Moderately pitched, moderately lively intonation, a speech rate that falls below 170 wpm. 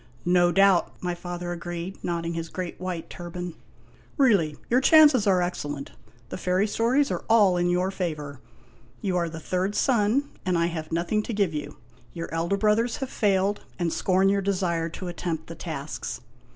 No: medium, 180 Hz; average, 3.0 semitones; average, 180 wpm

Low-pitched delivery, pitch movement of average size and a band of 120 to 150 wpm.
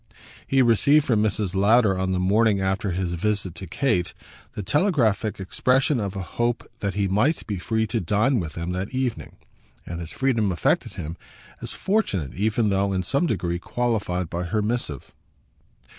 No: low, 100 Hz; average, 4.4 semitones; average, 175 wpm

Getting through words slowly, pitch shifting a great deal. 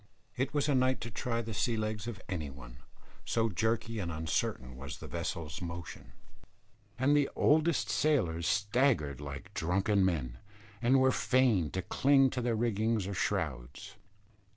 No: average, 150 wpm; wide, 7.7 semitones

